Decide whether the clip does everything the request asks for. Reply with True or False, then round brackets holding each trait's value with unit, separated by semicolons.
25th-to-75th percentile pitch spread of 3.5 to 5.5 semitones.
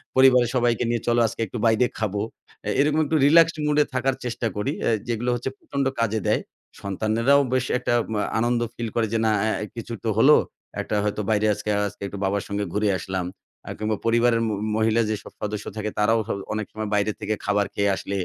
False (2.7 semitones)